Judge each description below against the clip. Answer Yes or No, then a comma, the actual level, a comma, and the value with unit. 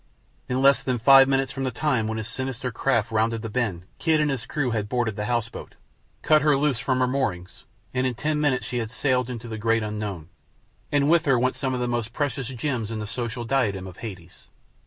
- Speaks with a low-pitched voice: Yes, low, 125 Hz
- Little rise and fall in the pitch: No, average, 3.4 semitones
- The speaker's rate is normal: No, fast, 235 wpm